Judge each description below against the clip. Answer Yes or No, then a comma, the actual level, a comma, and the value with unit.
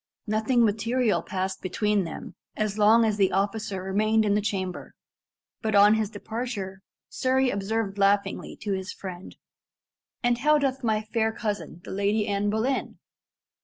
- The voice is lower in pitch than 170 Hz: No, high, 210 Hz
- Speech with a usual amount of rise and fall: No, narrow, 2.1 semitones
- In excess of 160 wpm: No, average, 150 wpm